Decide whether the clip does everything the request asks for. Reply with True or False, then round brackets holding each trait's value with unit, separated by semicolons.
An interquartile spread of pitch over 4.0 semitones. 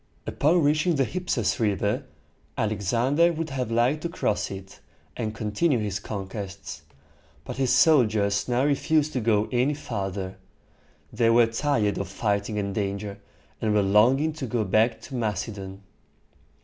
True (5.1 semitones)